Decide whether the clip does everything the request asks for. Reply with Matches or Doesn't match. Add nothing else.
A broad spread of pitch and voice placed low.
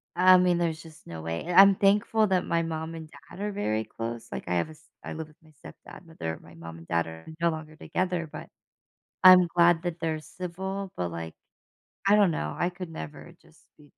Doesn't match